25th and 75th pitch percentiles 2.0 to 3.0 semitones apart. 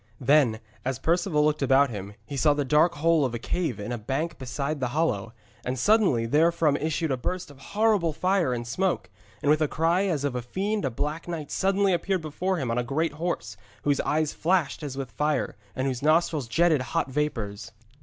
No: average, 4.6 semitones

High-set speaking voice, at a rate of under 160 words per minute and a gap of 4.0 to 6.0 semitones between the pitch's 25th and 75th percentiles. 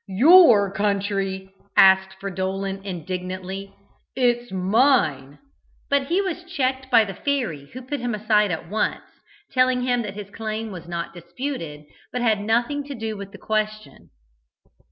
Yes: high, 210 Hz; average, 150 wpm; average, 4.7 semitones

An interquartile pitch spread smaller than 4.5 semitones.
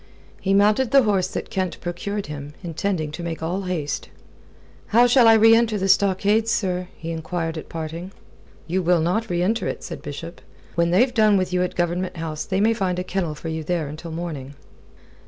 Yes: average, 3.7 semitones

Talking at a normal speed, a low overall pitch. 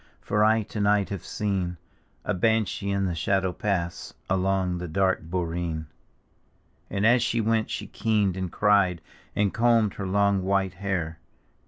Yes: average, 155 wpm; very low, 95 Hz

